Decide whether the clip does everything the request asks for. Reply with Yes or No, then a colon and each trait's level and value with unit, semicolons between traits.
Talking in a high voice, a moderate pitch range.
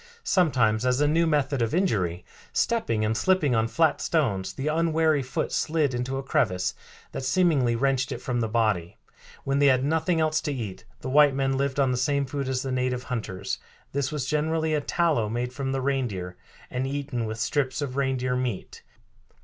No: low, 135 Hz; average, 3.7 semitones